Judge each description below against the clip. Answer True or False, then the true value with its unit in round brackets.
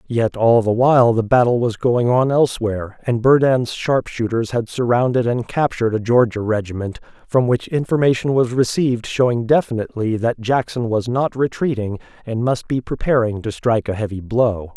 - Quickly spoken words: False (165 wpm)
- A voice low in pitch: True (120 Hz)